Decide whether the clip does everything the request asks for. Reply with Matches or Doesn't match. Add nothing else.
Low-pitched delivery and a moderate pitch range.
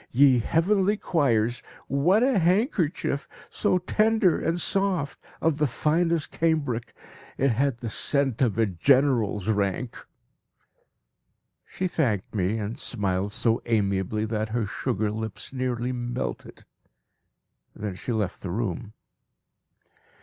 Doesn't match